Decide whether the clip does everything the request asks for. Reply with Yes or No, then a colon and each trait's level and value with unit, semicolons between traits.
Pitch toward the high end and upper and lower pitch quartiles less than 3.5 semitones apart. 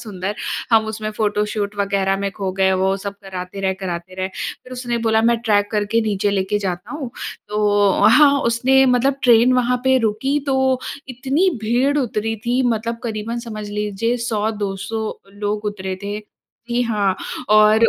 Yes: high, 215 Hz; average, 2.8 semitones